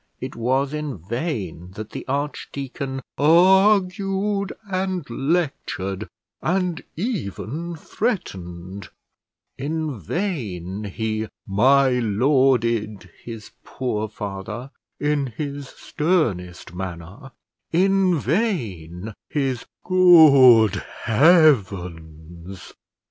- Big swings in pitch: Yes, wide, 8.3 semitones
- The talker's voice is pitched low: Yes, low, 130 Hz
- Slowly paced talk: Yes, slow, 80 wpm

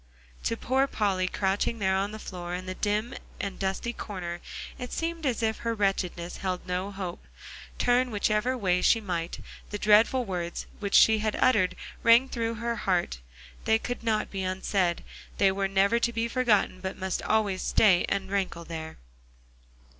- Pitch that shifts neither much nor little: Yes, average, 3.7 semitones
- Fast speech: No, average, 170 wpm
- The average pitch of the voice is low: No, high, 200 Hz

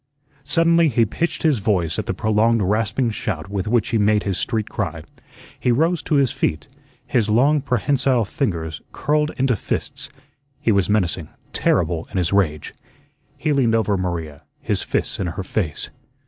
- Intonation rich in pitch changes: Yes, wide, 5.9 semitones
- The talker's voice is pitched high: No, low, 110 Hz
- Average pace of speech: Yes, average, 165 wpm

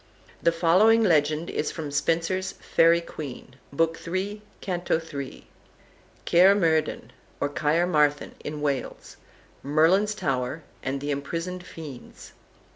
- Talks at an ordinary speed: No, slow, 115 wpm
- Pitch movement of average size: Yes, average, 3.6 semitones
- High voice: No, medium, 165 Hz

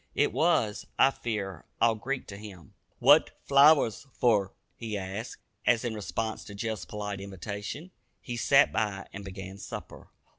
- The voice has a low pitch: Yes, low, 105 Hz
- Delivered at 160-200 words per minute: No, average, 150 wpm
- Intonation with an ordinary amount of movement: Yes, average, 3.1 semitones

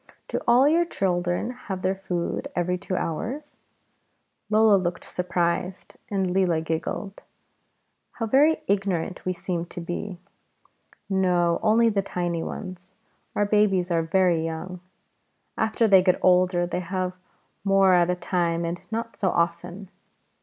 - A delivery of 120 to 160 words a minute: Yes, average, 140 wpm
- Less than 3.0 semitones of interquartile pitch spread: Yes, narrow, 2.4 semitones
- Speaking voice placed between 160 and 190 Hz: Yes, medium, 185 Hz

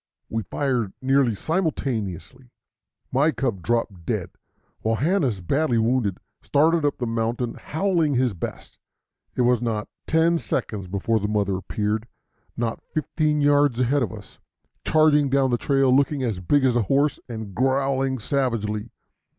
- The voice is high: No, low, 125 Hz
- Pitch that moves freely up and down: No, average, 4.5 semitones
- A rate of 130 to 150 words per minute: Yes, average, 145 wpm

